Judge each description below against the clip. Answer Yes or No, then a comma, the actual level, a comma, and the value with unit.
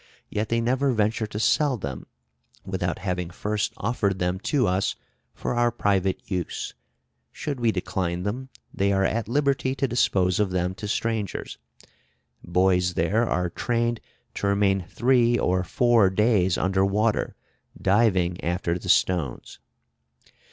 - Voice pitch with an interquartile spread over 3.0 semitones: Yes, average, 4.2 semitones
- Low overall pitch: Yes, low, 100 Hz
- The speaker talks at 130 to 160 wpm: Yes, average, 140 wpm